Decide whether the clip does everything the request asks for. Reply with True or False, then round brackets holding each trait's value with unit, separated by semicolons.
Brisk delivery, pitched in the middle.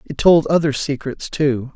False (170 wpm; 145 Hz)